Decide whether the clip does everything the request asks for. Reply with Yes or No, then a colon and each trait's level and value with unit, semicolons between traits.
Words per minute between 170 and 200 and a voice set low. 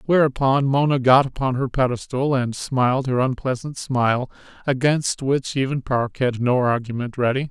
No: average, 150 wpm; low, 130 Hz